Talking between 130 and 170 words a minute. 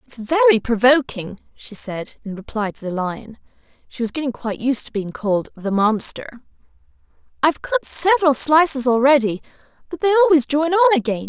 Yes: average, 165 wpm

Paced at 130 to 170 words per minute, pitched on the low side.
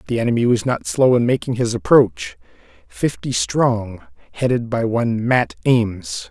Yes: average, 145 wpm; low, 120 Hz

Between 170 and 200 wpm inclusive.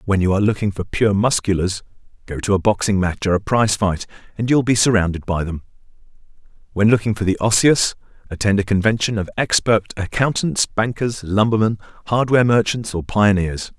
Yes: average, 175 wpm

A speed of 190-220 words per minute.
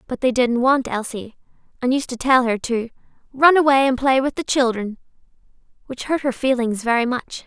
Yes: average, 195 wpm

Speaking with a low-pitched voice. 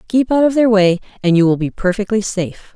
No: high, 205 Hz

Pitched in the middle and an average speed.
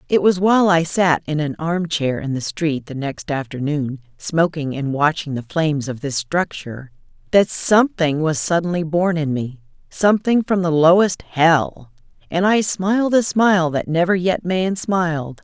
Yes: medium, 165 Hz; average, 175 wpm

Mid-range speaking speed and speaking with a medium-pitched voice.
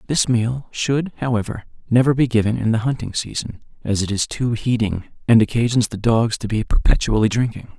No: average, 185 wpm; low, 115 Hz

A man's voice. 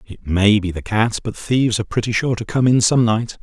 Yes: male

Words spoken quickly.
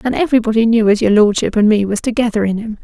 Yes: fast, 255 wpm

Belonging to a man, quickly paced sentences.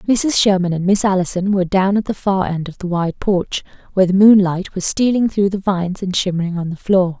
No: female; fast, 235 wpm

